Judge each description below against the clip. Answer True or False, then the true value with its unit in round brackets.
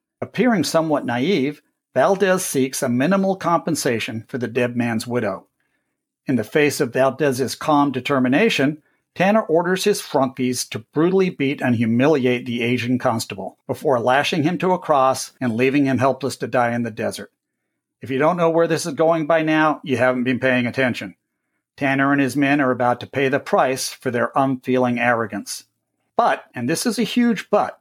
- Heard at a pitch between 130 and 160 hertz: True (135 Hz)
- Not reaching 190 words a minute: True (180 wpm)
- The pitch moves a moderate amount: True (3.9 semitones)